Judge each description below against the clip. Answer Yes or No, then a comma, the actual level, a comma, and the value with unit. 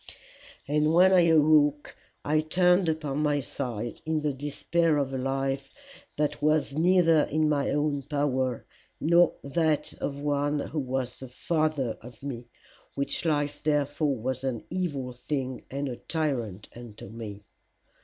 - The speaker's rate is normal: Yes, average, 150 wpm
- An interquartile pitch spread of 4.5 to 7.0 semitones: No, average, 2.8 semitones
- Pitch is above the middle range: No, medium, 145 Hz